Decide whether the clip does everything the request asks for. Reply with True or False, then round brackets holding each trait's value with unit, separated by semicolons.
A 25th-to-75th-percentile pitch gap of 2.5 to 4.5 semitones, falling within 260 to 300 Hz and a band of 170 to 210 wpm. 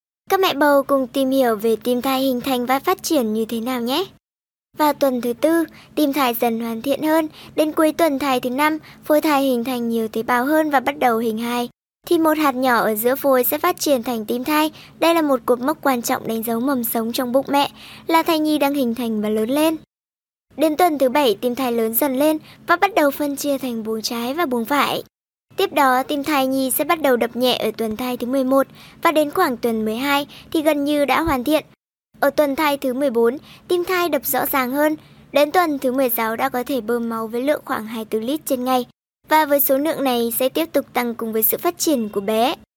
False (3.8 semitones; 270 Hz; 240 wpm)